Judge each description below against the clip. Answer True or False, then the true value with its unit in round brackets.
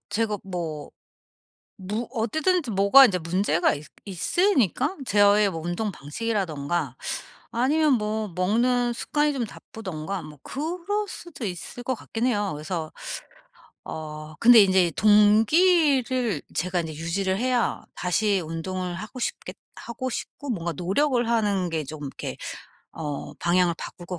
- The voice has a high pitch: True (200 Hz)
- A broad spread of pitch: True (5.9 semitones)